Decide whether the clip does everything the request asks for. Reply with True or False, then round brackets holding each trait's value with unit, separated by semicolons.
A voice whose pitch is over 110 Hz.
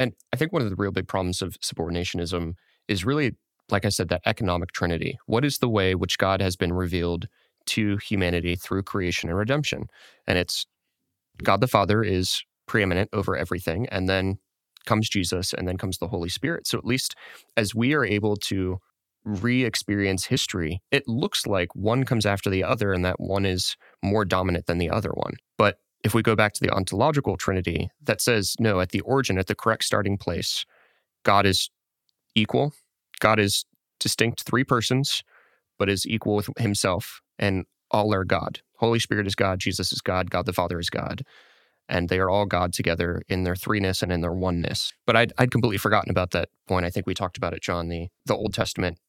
False (100 Hz)